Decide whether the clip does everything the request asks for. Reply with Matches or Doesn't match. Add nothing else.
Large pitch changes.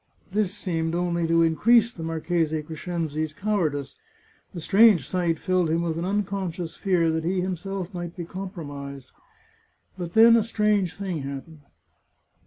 Doesn't match